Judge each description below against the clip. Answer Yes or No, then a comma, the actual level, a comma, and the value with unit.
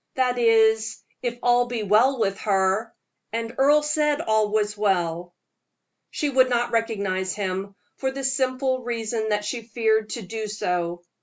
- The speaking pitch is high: Yes, high, 225 Hz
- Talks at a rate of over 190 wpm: No, average, 155 wpm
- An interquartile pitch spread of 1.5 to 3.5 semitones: Yes, average, 3.1 semitones